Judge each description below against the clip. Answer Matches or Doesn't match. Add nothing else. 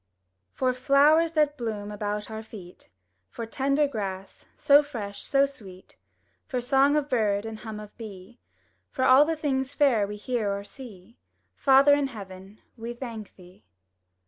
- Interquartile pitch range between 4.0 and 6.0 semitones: Matches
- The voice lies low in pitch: Doesn't match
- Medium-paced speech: Matches